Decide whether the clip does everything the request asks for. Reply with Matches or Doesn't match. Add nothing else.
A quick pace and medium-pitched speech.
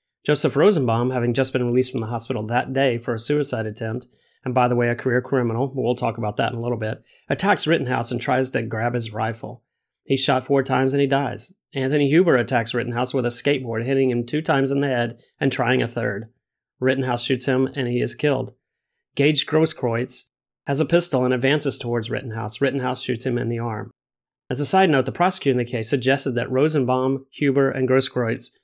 Doesn't match